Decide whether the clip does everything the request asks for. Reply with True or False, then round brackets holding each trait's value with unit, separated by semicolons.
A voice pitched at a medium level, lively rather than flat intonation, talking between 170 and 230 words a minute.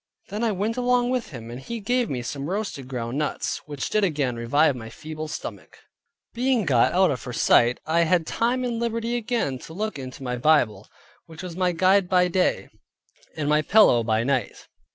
True (160 Hz; 8.8 semitones; 195 wpm)